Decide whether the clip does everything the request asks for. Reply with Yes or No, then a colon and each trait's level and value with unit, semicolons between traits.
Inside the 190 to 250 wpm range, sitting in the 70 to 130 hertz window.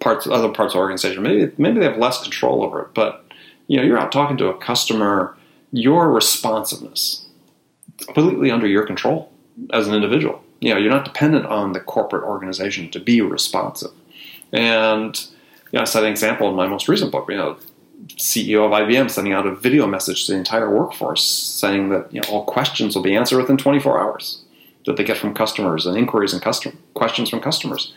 Yes: average, 200 wpm; low, 110 Hz